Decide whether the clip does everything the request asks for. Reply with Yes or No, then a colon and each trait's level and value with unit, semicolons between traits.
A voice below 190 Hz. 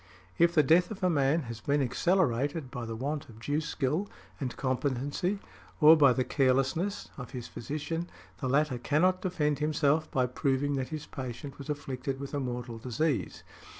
Yes: medium, 140 Hz